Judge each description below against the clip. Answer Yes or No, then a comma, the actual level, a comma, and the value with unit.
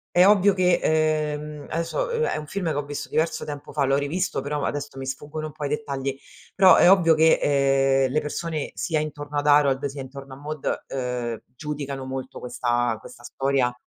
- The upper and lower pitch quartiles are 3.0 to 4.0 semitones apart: No, narrow, 2.5 semitones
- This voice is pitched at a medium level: Yes, medium, 145 Hz